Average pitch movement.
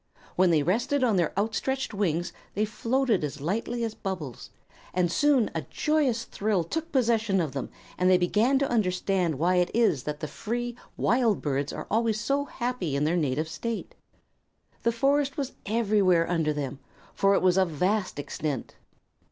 No: wide, 6.1 semitones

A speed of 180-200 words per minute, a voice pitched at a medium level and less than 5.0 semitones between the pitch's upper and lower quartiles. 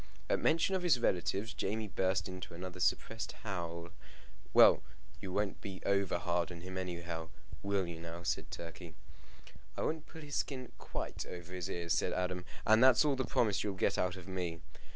No: average, 185 wpm; very low, 95 Hz; average, 3.9 semitones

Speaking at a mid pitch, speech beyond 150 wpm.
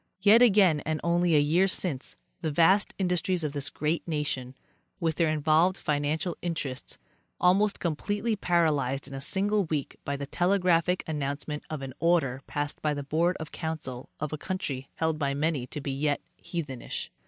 Yes: medium, 155 Hz; average, 170 wpm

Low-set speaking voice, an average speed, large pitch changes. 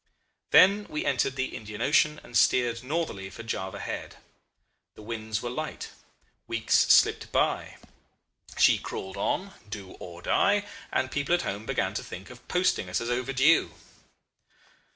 Yes: low, 125 Hz; average, 150 wpm; wide, 6.4 semitones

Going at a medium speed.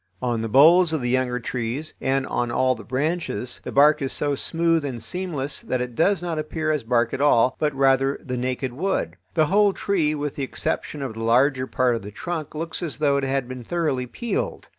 No: fast, 220 wpm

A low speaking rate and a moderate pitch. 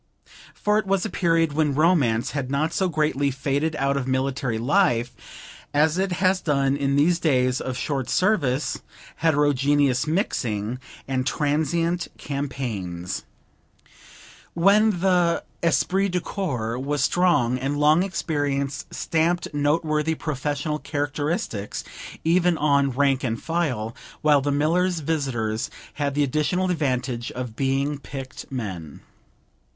Yes: slow, 125 wpm; medium, 145 Hz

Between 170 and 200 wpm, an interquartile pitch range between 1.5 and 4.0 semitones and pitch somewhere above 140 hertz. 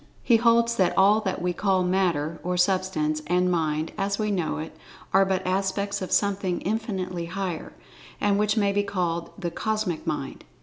Yes: average, 175 wpm; narrow, 2.4 semitones; high, 190 Hz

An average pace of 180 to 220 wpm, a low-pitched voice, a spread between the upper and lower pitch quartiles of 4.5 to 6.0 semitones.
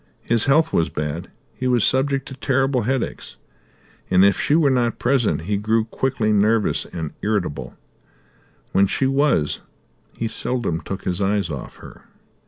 No: average, 155 wpm; low, 115 Hz; average, 5.3 semitones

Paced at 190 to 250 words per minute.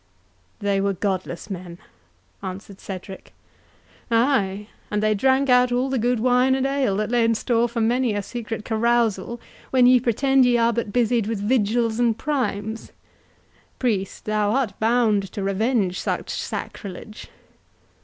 No: average, 145 wpm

